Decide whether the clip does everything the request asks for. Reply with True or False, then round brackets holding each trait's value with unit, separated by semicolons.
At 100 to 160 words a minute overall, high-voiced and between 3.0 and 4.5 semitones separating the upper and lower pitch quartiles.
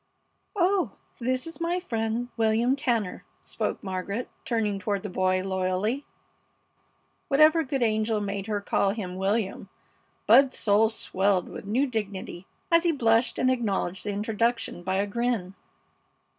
True (145 wpm; 220 Hz; 4.1 semitones)